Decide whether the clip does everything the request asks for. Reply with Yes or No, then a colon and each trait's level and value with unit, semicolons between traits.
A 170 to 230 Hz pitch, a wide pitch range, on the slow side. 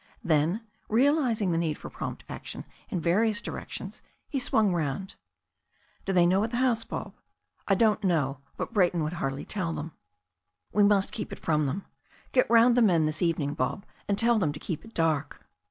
No: medium, 185 Hz; wide, 5.7 semitones; average, 190 wpm